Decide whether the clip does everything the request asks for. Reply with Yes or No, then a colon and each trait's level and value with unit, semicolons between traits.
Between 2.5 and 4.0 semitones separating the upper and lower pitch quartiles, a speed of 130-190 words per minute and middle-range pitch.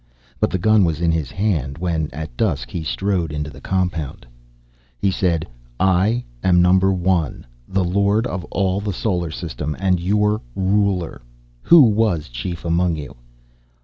No: average, 3.3 semitones; average, 155 wpm; very low, 90 Hz